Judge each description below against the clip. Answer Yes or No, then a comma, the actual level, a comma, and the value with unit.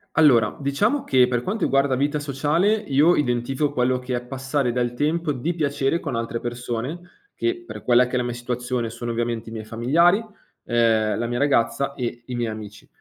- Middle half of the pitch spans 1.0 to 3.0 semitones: No, average, 3.4 semitones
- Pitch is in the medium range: No, low, 125 Hz